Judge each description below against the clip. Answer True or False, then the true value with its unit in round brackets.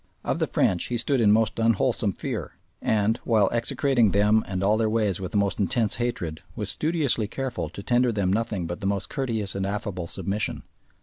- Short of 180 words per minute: False (195 wpm)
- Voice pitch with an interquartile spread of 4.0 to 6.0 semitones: False (3.1 semitones)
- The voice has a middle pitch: False (105 Hz)